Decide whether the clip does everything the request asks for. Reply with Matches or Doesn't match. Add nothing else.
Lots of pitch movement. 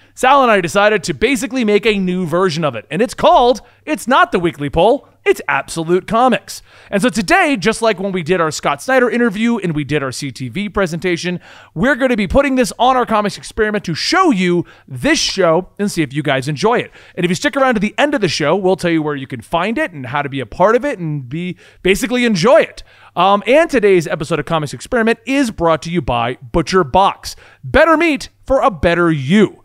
Matches